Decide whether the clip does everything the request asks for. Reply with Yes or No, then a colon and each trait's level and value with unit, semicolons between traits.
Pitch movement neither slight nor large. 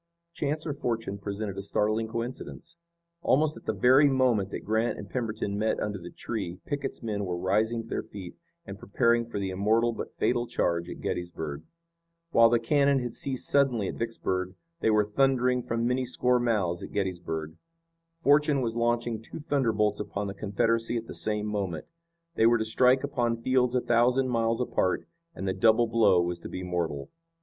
Yes: average, 3.8 semitones